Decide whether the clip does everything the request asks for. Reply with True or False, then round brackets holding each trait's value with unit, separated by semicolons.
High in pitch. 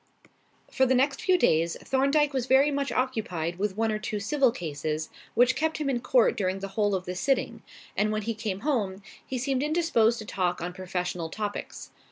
True (220 Hz)